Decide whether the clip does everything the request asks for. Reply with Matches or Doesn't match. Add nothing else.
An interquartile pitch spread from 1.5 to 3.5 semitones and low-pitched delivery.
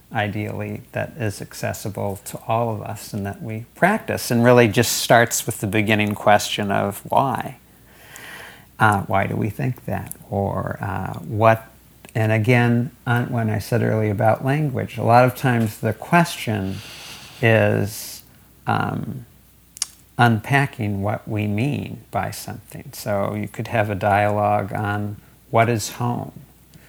Matches